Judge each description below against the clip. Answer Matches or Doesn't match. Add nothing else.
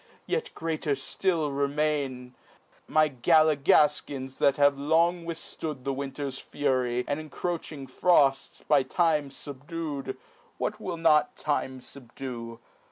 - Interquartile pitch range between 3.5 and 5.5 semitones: Doesn't match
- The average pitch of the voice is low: Doesn't match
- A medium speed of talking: Doesn't match